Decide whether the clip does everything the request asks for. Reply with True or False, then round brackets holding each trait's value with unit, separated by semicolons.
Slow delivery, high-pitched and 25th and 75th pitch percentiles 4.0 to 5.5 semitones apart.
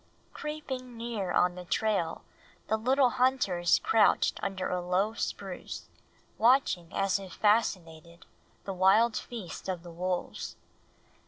True (120 wpm; 195 Hz; 4.7 semitones)